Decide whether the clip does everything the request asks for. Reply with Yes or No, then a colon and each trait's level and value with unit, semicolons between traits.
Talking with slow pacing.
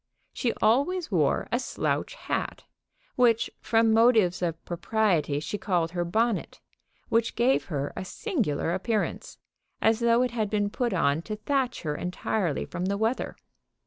No: average, 150 wpm